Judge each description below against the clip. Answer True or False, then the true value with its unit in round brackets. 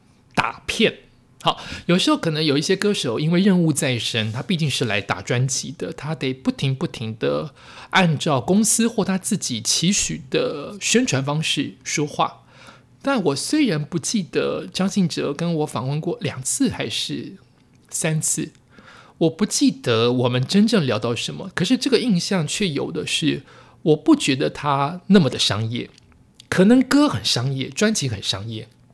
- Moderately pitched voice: True (160 Hz)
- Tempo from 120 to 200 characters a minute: False (240 characters per minute)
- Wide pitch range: True (6.8 semitones)